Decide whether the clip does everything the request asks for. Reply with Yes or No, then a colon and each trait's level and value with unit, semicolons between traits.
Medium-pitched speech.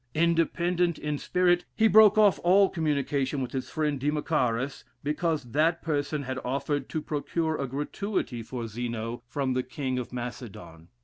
Yes: medium, 145 Hz